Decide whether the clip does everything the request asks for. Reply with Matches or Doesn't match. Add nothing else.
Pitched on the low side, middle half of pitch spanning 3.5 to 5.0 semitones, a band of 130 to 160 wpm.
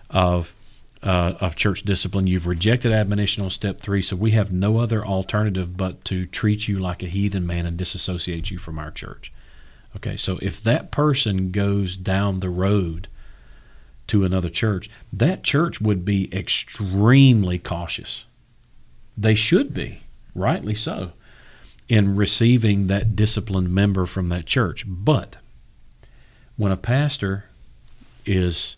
Doesn't match